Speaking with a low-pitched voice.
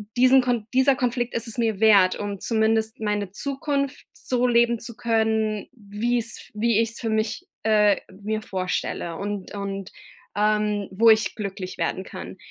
No: high, 220 Hz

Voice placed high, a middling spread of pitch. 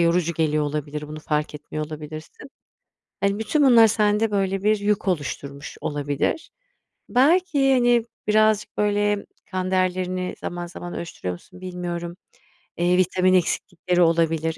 No: medium, 180 Hz; average, 4.7 semitones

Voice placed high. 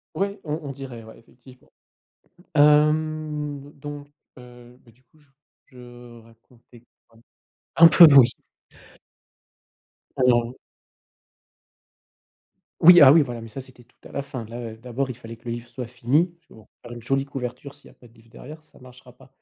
No: low, 125 Hz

